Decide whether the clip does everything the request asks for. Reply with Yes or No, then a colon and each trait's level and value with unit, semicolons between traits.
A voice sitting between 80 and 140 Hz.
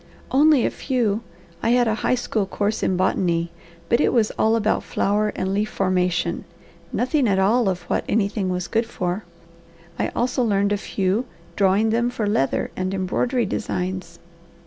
No: high, 205 Hz